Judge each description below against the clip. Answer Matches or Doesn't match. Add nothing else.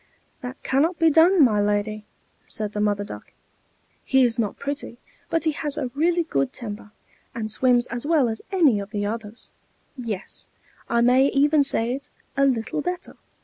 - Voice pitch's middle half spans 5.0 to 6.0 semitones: Matches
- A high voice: Matches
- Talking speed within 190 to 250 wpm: Doesn't match